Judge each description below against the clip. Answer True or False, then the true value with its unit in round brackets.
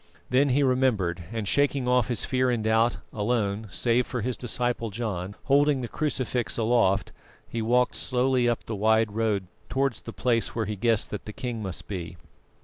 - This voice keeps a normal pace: True (180 wpm)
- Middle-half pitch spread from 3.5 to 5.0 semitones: False (2.8 semitones)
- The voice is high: False (115 Hz)